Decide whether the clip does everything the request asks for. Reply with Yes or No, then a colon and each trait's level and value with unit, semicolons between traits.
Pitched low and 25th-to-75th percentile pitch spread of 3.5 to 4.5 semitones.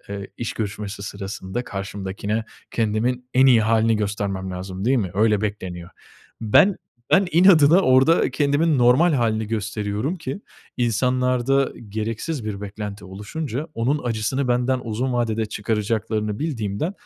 Yes: low, 110 Hz; average, 4.1 semitones